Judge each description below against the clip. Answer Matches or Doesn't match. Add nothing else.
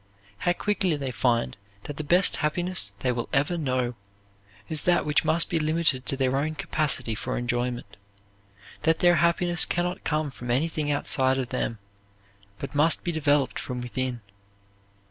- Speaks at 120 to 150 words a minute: Doesn't match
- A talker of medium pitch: Matches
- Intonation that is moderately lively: Matches